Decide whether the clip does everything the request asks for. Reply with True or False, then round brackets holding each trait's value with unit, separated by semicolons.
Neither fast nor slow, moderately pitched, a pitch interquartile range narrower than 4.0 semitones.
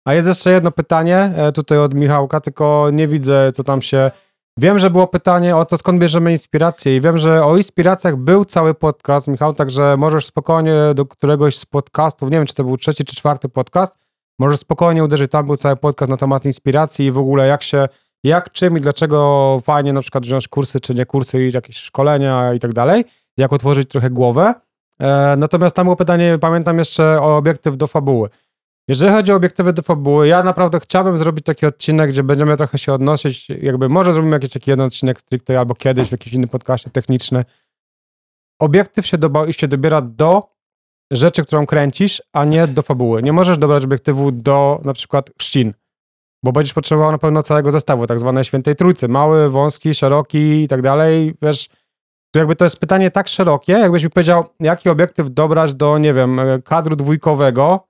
False (190 wpm; 150 Hz; 3.3 semitones)